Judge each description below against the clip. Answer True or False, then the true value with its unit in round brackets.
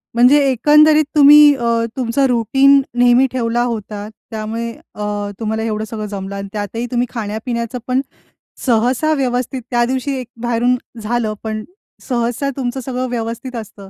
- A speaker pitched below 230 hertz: False (240 Hz)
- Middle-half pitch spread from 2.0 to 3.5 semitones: True (2.7 semitones)